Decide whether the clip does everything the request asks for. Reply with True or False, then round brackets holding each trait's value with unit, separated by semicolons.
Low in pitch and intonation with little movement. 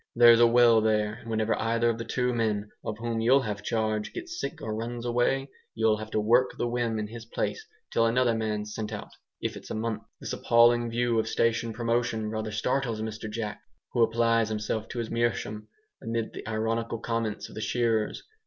True (115 Hz; 1.4 semitones)